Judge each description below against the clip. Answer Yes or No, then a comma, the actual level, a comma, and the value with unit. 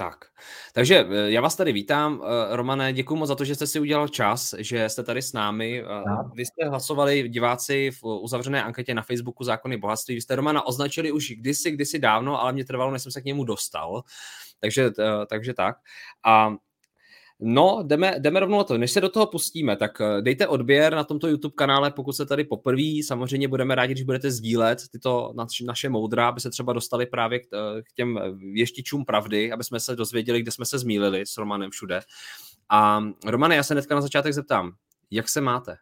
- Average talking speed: No, fast, 190 wpm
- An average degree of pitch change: Yes, average, 4.0 semitones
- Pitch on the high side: No, low, 125 Hz